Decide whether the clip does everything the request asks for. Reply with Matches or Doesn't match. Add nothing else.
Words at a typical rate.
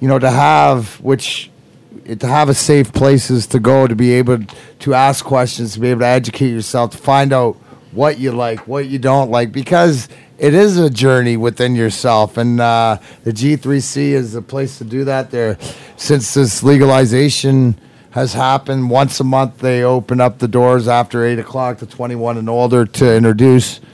Matches